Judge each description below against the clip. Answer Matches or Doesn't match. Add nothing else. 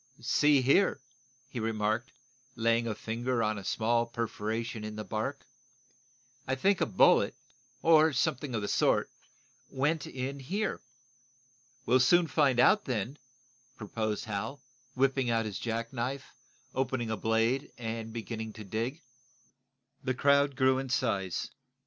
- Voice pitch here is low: Matches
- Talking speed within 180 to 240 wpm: Doesn't match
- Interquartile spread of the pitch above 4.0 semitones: Doesn't match